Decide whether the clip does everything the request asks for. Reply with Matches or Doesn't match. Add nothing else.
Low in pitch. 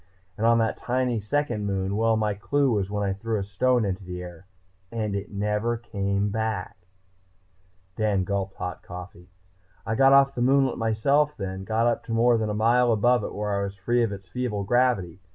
Matches